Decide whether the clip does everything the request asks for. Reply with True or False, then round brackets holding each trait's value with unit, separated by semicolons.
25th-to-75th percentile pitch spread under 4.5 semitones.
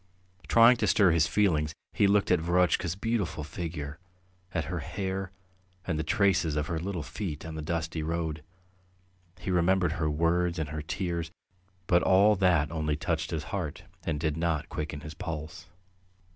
True (2.9 semitones)